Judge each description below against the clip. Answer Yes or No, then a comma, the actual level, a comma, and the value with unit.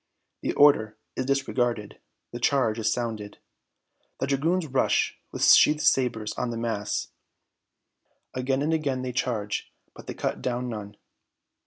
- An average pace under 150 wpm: Yes, average, 140 wpm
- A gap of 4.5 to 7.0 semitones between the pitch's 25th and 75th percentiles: No, average, 3.7 semitones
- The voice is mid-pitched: No, low, 125 Hz